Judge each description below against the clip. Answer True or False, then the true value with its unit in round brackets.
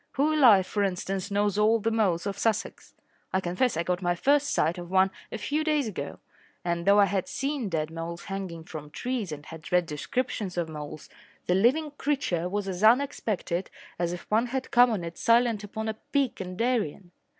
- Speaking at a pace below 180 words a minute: False (200 wpm)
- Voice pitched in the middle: False (200 Hz)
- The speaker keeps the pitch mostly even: False (5.3 semitones)